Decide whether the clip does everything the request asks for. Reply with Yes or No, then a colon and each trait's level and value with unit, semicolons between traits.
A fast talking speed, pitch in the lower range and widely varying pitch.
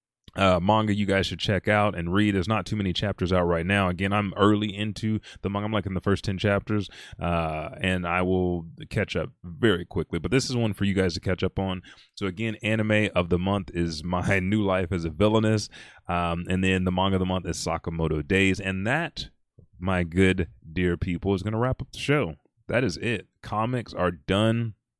No: fast, 220 wpm; very low, 95 Hz; average, 2.7 semitones